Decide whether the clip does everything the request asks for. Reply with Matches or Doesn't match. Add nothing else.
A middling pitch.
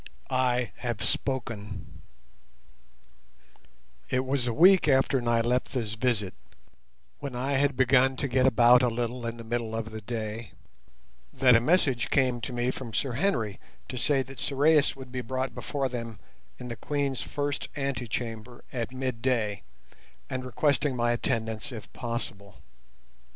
Doesn't match